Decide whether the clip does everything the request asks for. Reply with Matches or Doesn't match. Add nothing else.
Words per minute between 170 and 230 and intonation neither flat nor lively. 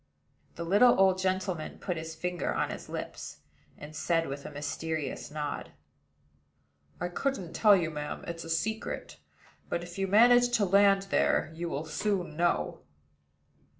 Doesn't match